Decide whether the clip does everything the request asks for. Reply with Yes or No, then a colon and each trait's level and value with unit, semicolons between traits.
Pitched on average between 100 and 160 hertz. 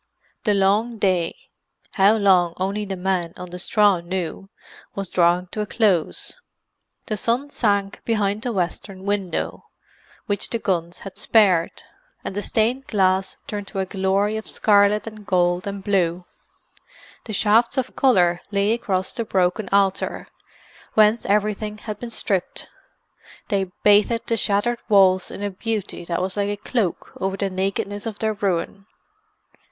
No: high, 200 Hz